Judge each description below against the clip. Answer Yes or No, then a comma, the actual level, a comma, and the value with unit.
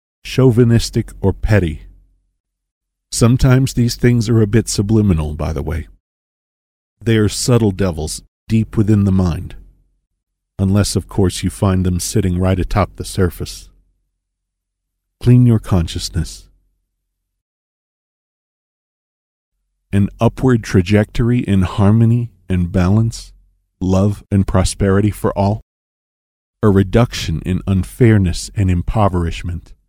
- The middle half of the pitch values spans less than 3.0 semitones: No, average, 3.3 semitones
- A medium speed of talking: No, slow, 105 wpm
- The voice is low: Yes, very low, 95 Hz